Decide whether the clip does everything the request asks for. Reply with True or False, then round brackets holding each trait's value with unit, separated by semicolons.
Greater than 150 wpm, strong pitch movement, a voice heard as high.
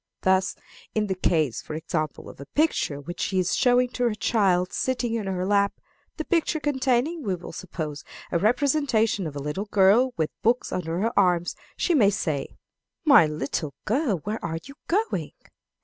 True (180 wpm; 6.5 semitones; 200 Hz)